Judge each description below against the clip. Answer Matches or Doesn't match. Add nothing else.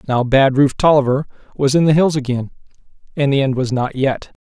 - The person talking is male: Matches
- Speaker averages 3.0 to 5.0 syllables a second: Doesn't match